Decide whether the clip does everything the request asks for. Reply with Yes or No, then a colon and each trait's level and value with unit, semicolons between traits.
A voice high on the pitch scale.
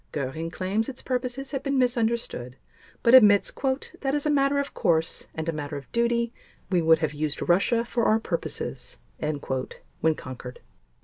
Yes: high, 205 Hz